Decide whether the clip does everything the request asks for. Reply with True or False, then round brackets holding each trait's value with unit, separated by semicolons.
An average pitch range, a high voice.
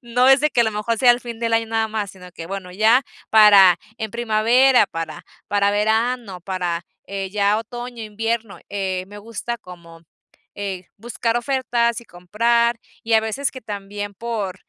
True (3.2 semitones; 220 Hz)